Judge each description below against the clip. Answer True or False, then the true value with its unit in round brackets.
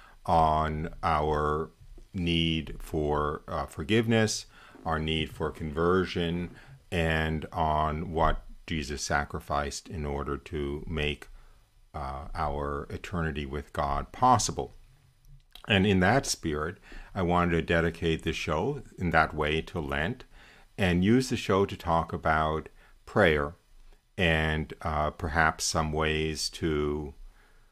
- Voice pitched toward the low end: True (80 Hz)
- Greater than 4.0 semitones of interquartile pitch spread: False (3.5 semitones)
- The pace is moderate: False (115 wpm)